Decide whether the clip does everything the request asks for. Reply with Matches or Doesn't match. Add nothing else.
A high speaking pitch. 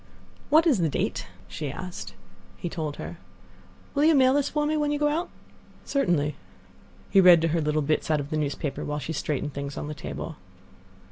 Doesn't match